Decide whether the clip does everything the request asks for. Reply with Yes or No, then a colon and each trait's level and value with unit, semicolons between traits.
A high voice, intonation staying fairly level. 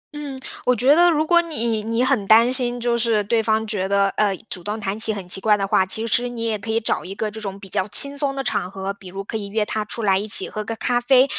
No: high, 220 Hz; average, 3.4 semitones